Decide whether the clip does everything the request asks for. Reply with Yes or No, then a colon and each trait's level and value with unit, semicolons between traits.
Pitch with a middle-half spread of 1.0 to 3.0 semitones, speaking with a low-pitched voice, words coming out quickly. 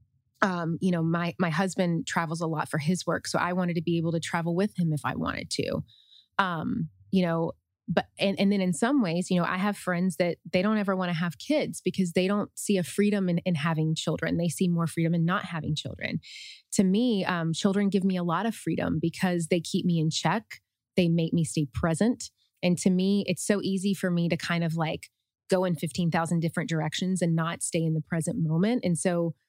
No: narrow, 2.4 semitones; medium, 175 Hz; fast, 235 wpm